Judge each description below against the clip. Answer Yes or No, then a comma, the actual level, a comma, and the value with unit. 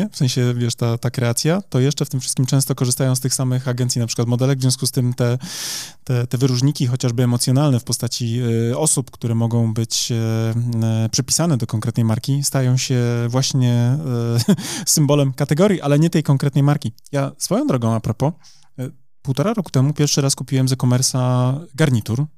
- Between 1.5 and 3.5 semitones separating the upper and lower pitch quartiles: Yes, average, 2.8 semitones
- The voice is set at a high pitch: No, low, 130 Hz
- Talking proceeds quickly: Yes, fast, 185 wpm